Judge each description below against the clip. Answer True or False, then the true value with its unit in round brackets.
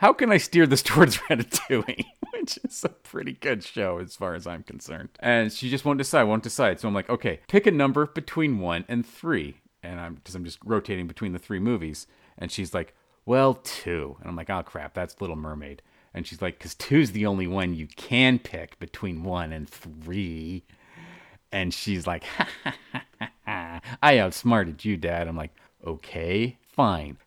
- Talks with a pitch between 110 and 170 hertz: False (95 Hz)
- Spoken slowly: False (200 wpm)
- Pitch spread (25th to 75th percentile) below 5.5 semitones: False (6.0 semitones)